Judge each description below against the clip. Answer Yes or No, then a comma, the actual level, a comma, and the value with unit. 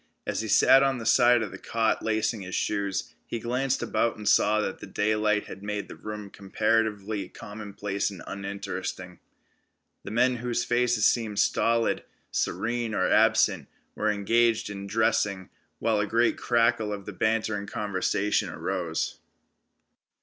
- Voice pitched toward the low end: Yes, low, 105 Hz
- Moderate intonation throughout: No, narrow, 2.3 semitones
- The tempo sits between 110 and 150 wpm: Yes, average, 140 wpm